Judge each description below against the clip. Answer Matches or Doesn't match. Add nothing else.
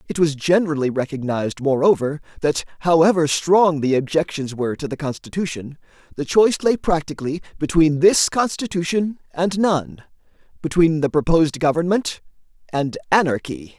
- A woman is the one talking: Doesn't match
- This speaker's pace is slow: Matches